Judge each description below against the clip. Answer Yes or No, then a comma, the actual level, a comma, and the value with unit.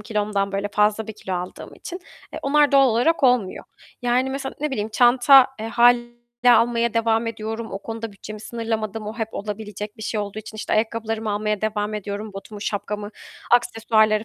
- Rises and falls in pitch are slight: Yes, narrow, 2.2 semitones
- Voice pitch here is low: No, high, 220 Hz